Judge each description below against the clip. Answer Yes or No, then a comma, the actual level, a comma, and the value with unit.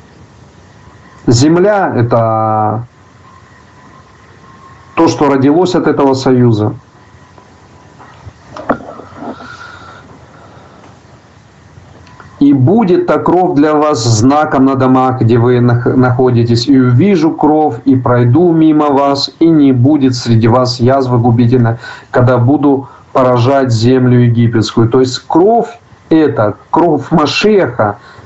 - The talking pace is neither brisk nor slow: No, slow, 95 wpm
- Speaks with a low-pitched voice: Yes, low, 125 Hz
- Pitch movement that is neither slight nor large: Yes, average, 3.6 semitones